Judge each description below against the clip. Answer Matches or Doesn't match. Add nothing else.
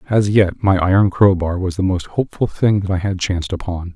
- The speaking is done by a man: Matches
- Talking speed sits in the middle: Doesn't match